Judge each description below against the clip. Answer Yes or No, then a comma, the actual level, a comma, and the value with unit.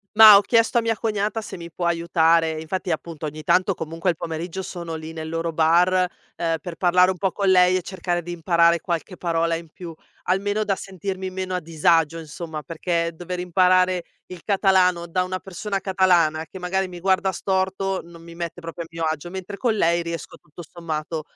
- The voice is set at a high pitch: No, medium, 175 Hz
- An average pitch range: No, narrow, 2.2 semitones